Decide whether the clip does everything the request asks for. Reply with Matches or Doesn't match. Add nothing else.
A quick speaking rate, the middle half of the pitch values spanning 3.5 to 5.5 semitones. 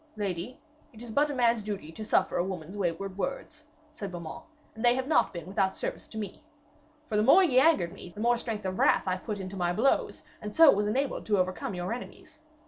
Matches